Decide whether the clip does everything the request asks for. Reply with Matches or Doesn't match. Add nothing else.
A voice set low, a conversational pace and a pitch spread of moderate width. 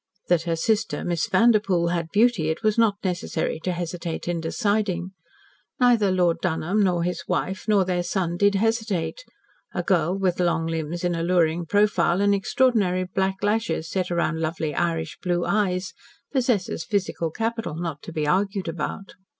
Doesn't match